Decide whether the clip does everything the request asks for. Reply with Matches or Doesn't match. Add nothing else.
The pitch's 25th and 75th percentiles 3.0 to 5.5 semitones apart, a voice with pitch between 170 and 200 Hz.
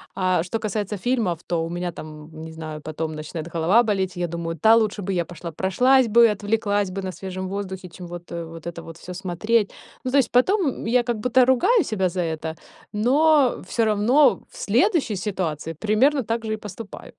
Matches